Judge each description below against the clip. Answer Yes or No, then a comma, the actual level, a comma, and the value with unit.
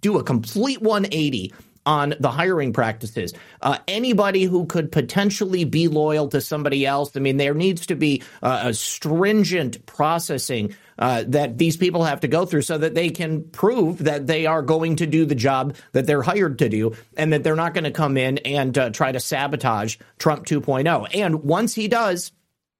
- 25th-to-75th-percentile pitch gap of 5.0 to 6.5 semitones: No, average, 3.5 semitones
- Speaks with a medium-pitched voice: Yes, medium, 155 Hz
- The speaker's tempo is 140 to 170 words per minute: No, average, 190 wpm